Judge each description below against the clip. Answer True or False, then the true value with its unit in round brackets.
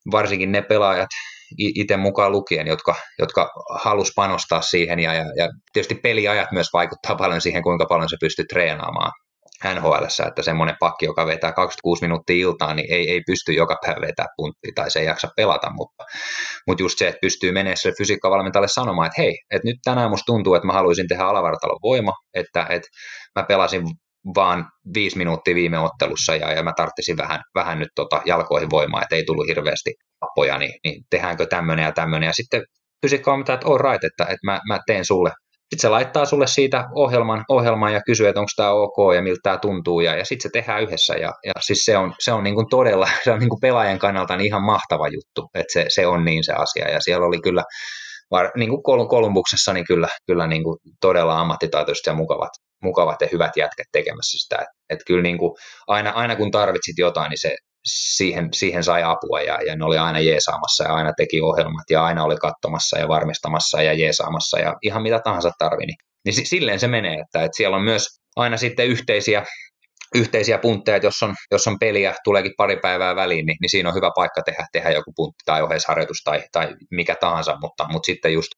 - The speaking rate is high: True (205 wpm)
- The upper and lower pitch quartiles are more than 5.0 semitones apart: True (5.5 semitones)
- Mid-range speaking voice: False (100 Hz)